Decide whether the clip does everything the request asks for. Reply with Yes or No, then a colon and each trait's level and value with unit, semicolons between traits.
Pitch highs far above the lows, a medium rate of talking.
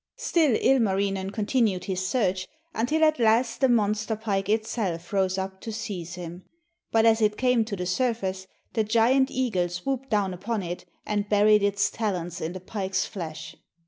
No: average, 3.4 semitones; average, 170 wpm